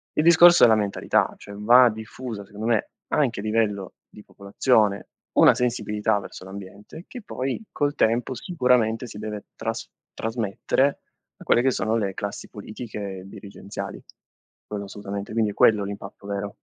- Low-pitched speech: Yes, low, 110 Hz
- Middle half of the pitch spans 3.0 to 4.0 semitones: Yes, average, 3.3 semitones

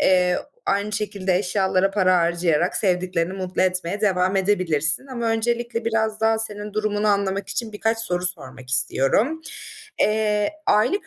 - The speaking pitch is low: No, high, 200 Hz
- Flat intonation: No, average, 3.2 semitones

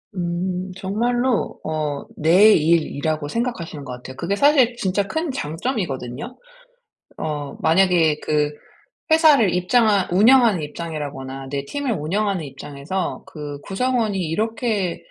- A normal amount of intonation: No, wide, 6.8 semitones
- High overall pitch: No, medium, 180 Hz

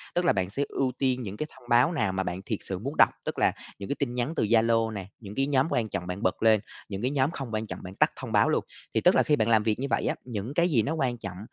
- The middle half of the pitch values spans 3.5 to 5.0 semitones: Yes, average, 4.7 semitones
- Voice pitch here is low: Yes, low, 115 Hz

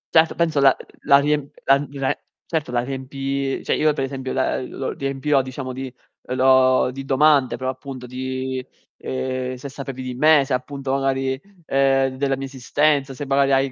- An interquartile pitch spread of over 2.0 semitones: No, narrow, 1.2 semitones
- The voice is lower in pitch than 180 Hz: Yes, low, 135 Hz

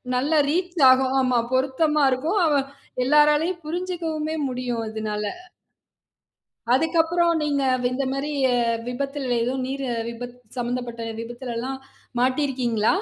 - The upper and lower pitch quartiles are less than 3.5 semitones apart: No, average, 3.9 semitones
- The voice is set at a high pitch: Yes, very high, 270 Hz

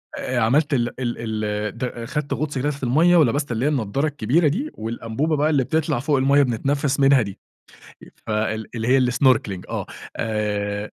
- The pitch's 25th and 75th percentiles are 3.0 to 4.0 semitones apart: No, average, 4.6 semitones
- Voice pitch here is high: No, low, 130 Hz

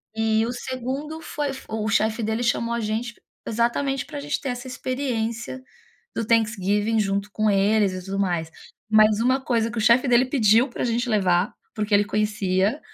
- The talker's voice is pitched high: Yes, high, 225 Hz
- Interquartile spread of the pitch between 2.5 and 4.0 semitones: Yes, average, 2.8 semitones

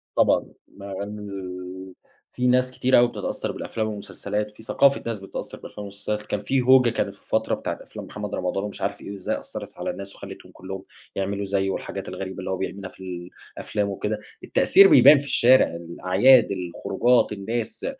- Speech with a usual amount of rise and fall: Yes, average, 3.6 semitones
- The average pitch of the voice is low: Yes, low, 100 Hz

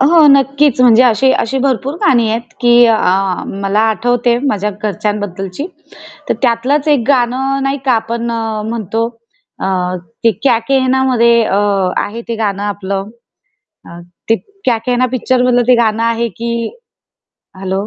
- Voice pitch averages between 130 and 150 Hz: No, high, 235 Hz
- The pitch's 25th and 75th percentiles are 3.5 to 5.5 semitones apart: No, average, 3.1 semitones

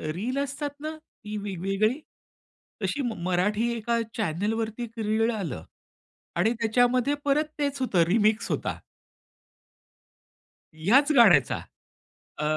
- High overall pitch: Yes, high, 225 Hz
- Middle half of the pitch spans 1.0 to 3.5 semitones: No, average, 4.4 semitones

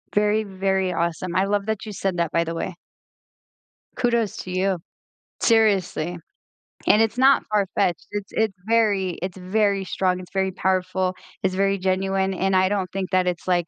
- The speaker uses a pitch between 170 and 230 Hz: Yes, high, 190 Hz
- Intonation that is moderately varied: No, narrow, 2.0 semitones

